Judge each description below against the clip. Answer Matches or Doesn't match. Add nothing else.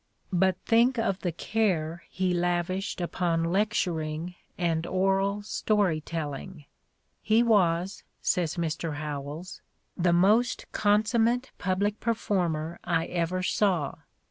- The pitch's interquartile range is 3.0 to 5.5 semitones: Matches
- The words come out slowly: Matches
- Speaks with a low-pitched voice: Doesn't match